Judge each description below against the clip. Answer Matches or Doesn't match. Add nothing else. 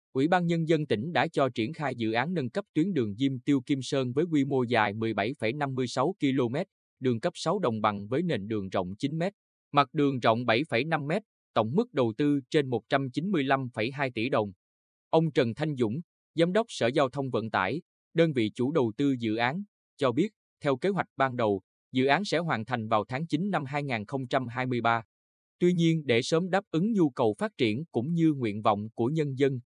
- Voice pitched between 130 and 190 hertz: Matches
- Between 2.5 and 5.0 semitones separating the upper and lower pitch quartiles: Doesn't match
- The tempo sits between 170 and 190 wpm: Doesn't match